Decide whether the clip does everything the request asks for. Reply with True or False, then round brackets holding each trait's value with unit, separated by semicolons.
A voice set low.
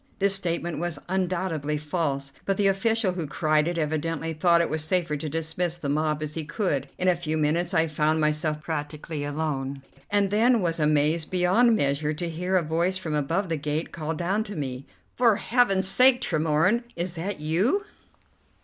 False (165 Hz)